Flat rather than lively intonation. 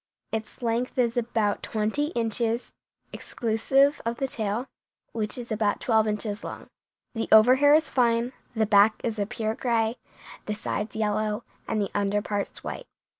Yes: narrow, 2.2 semitones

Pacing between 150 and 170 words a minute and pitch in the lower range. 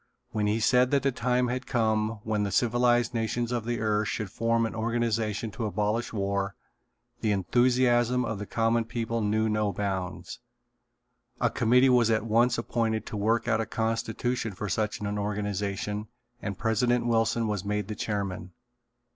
Yes: average, 165 wpm; low, 110 Hz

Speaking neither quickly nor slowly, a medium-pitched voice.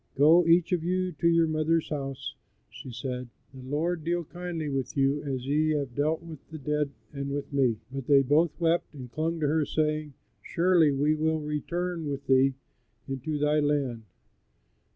Yes: average, 175 wpm; medium, 150 Hz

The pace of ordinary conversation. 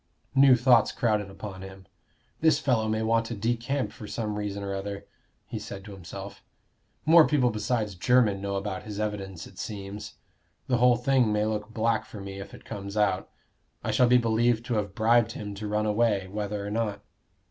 Yes: average, 190 wpm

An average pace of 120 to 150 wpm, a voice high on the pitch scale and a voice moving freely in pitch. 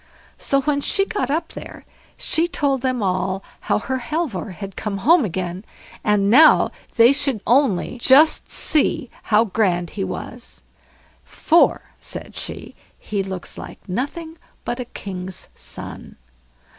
Yes: average, 140 wpm; high, 235 Hz; wide, 6.6 semitones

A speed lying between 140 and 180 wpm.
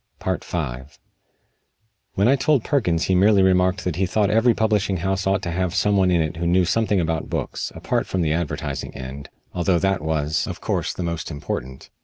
No: average, 195 wpm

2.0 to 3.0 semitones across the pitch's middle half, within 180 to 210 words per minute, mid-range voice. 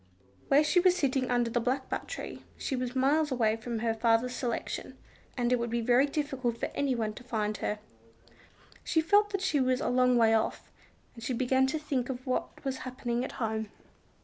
No: narrow, 2.5 semitones; average, 200 wpm; very high, 250 Hz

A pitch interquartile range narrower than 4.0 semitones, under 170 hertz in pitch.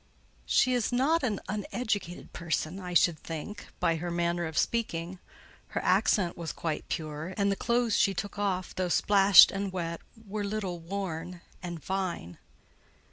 No: average, 3.2 semitones; medium, 185 Hz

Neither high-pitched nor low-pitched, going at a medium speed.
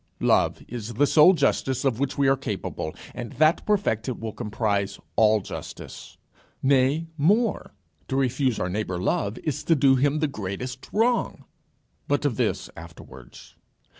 No: low, 130 Hz; average, 150 wpm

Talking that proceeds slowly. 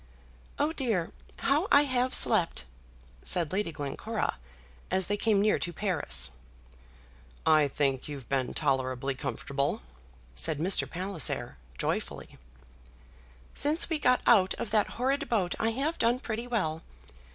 Yes: slow, 130 wpm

